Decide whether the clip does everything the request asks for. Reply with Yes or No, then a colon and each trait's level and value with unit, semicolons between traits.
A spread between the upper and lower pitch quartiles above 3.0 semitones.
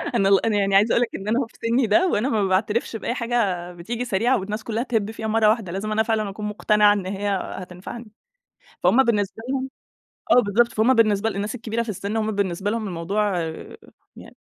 No: narrow, 2.6 semitones